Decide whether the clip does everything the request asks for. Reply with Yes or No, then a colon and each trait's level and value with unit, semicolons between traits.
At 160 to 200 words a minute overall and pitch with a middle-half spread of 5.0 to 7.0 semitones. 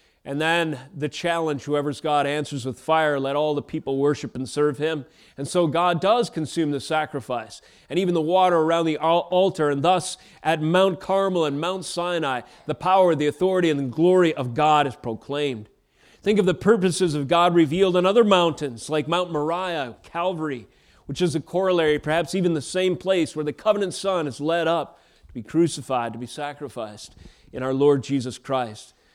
No: average, 185 wpm; average, 3.7 semitones